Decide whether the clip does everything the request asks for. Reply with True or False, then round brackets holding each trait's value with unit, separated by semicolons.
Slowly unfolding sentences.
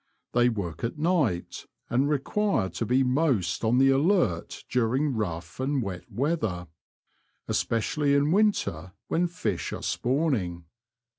True (130 wpm)